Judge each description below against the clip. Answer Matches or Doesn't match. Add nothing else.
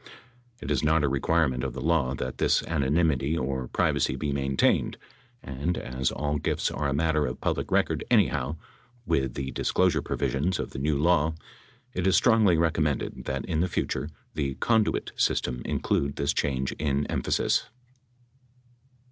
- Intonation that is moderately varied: Matches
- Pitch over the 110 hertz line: Doesn't match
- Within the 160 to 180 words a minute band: Matches